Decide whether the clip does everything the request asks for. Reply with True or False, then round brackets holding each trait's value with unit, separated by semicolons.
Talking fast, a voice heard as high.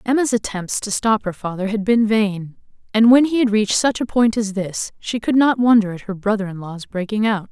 True (225 wpm; 215 Hz)